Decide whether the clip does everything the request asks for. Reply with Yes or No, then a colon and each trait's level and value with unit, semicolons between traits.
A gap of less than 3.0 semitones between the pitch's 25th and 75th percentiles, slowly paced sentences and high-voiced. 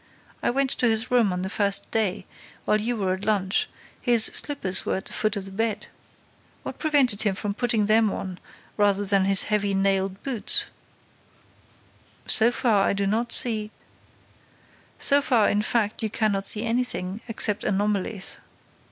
No: narrow, 2.6 semitones; average, 165 wpm; high, 210 Hz